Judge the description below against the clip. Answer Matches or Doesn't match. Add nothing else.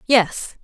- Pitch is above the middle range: Matches